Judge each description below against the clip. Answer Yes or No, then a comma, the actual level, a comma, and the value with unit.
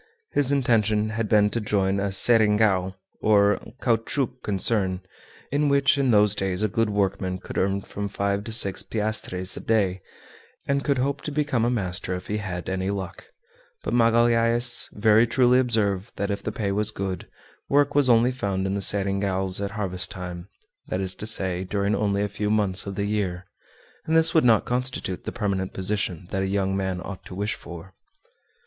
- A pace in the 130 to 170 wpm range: No, average, 185 wpm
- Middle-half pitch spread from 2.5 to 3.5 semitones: Yes, average, 3.2 semitones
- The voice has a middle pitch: No, low, 105 Hz